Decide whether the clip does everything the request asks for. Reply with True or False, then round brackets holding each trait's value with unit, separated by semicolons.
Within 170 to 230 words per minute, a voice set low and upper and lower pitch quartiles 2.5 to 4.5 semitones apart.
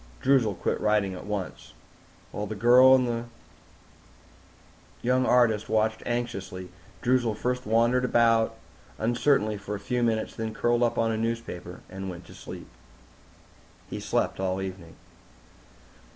False (140 wpm; 115 Hz; 3.0 semitones)